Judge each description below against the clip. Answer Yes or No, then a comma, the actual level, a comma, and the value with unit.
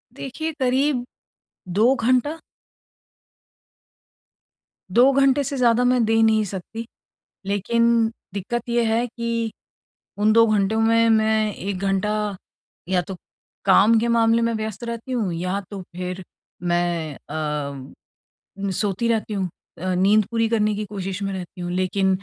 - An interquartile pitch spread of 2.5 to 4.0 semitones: Yes, average, 3.5 semitones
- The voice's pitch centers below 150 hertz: No, high, 220 Hz